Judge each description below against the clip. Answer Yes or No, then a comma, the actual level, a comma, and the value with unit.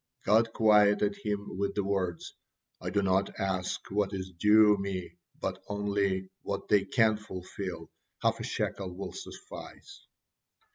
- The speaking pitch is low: Yes, low, 100 Hz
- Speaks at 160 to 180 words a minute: No, average, 140 wpm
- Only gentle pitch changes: Yes, narrow, 1.8 semitones